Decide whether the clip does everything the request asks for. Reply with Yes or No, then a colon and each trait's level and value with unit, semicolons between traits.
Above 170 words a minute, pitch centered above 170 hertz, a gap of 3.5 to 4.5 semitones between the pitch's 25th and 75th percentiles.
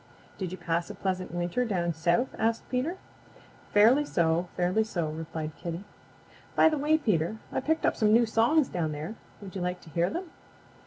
No: average, 190 wpm; medium, 185 Hz; wide, 5.6 semitones